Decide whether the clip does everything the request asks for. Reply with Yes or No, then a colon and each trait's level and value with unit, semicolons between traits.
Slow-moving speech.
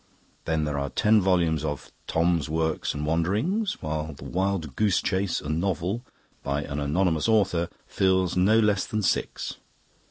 No: average, 155 wpm